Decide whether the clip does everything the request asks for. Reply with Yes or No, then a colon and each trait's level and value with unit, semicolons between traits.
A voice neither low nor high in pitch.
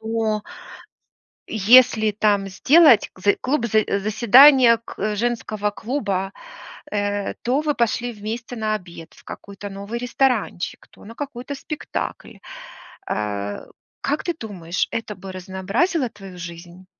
No: high, 215 Hz